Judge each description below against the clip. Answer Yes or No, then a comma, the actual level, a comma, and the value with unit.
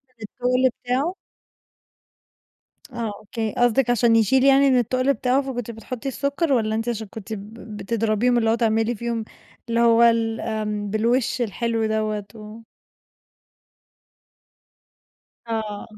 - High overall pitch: Yes, high, 230 Hz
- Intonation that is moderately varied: No, narrow, 2.3 semitones